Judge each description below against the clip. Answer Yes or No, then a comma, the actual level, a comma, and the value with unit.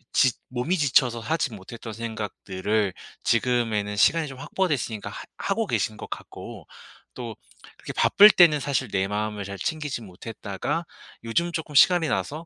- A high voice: No, low, 120 Hz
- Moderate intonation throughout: No, wide, 6.2 semitones